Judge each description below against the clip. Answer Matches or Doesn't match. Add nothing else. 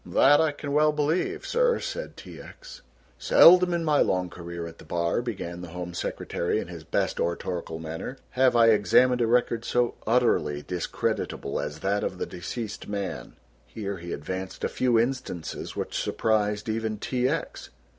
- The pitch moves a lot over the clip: Matches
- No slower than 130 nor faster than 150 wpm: Doesn't match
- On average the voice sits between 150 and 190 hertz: Doesn't match